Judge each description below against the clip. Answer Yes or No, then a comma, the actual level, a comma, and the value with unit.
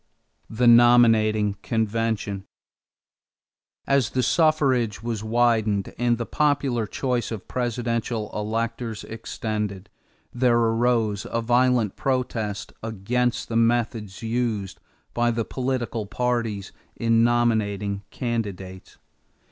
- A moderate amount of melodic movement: No, narrow, 2.2 semitones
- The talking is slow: Yes, slow, 100 wpm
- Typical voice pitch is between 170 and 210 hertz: No, low, 115 Hz